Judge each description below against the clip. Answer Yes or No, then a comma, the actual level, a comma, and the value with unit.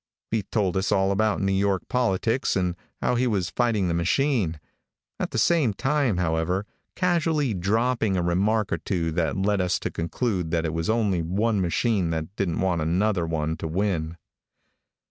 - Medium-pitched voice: No, very low, 95 Hz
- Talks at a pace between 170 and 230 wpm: Yes, average, 175 wpm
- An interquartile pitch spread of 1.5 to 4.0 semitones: No, average, 4.7 semitones